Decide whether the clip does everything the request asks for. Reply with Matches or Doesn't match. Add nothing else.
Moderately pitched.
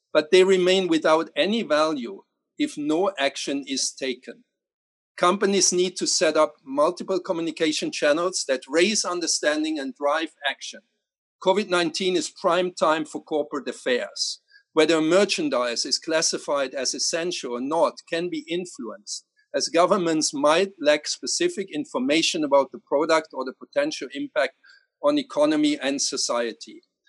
Matches